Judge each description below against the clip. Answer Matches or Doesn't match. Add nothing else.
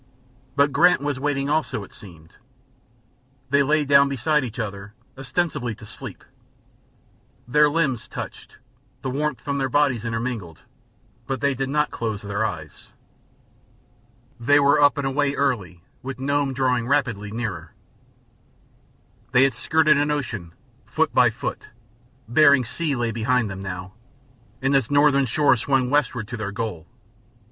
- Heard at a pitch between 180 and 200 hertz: Doesn't match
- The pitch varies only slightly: Doesn't match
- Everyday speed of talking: Matches